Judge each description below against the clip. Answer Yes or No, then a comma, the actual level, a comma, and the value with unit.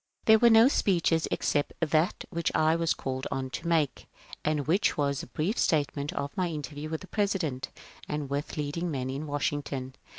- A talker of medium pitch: Yes, medium, 155 Hz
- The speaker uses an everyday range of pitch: Yes, average, 3.0 semitones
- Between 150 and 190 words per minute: Yes, average, 185 wpm